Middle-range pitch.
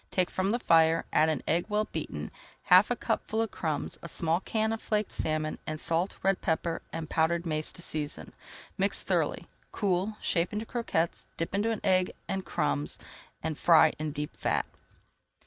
Yes: medium, 170 Hz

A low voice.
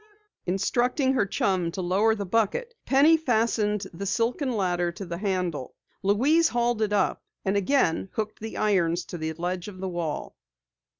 No: high, 200 Hz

